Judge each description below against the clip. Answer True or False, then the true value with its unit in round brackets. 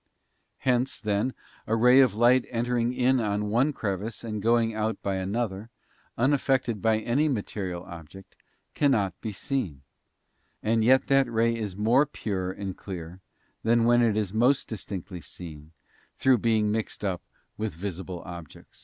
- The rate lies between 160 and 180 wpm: False (150 wpm)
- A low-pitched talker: True (110 Hz)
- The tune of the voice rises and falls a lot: False (3.8 semitones)